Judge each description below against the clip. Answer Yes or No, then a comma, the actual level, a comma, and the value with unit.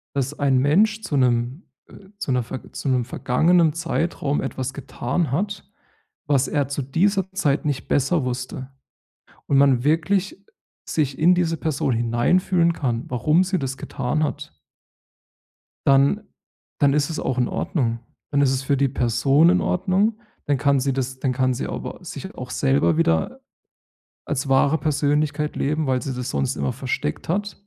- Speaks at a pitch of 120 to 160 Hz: Yes, medium, 140 Hz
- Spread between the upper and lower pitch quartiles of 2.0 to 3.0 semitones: No, average, 4.1 semitones